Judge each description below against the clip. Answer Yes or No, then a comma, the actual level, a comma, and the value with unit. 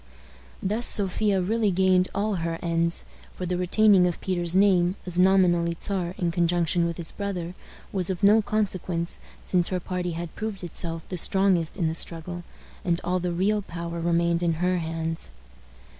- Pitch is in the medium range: Yes, medium, 180 Hz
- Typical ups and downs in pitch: No, narrow, 2.0 semitones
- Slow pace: No, average, 170 wpm